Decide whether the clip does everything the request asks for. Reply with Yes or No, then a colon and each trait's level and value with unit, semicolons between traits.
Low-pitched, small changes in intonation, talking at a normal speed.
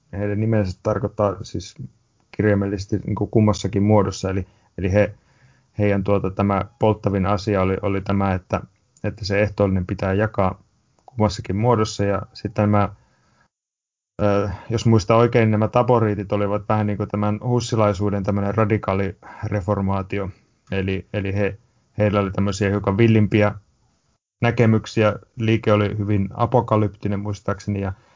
Yes: low, 105 Hz; narrow, 1.6 semitones; average, 130 wpm